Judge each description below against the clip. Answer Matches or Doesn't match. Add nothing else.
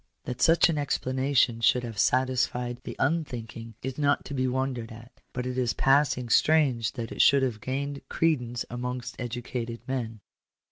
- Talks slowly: Doesn't match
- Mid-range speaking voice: Doesn't match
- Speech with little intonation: Matches